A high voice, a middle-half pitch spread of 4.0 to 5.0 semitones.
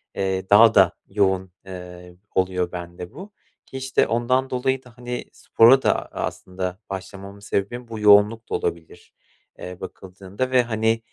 No: low, 100 Hz; average, 4.4 semitones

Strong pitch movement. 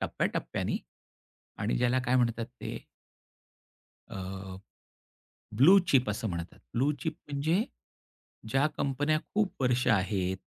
Yes: wide, 5.7 semitones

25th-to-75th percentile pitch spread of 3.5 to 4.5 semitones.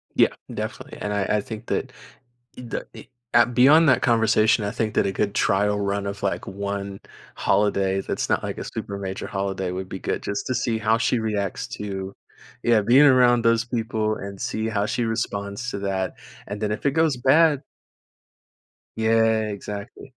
No: average, 2.8 semitones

